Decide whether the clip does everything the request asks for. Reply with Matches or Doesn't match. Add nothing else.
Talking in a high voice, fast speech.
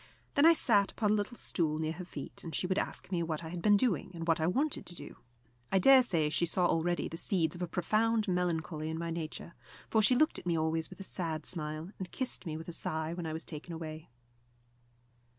Doesn't match